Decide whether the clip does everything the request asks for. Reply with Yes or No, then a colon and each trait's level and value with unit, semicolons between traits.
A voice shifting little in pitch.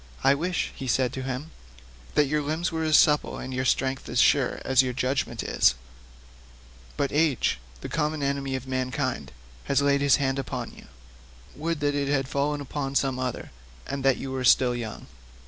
Yes: narrow, 1.9 semitones